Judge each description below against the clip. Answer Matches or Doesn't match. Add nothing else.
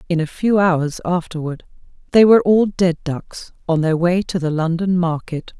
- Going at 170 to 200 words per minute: Matches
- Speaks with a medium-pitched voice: Matches